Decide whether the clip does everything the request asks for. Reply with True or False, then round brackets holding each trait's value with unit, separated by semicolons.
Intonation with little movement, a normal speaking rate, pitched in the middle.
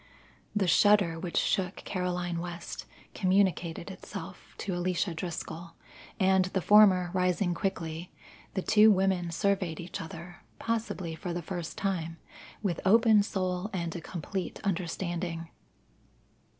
False (2.2 semitones; 125 wpm; 180 Hz)